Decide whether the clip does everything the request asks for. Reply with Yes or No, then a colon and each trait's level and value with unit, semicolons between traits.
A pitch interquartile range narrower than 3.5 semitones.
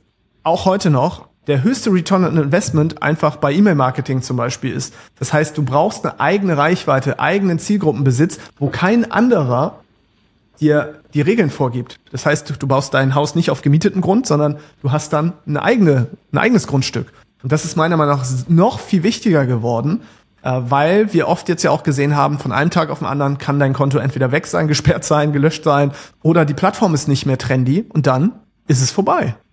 No: average, 3.8 semitones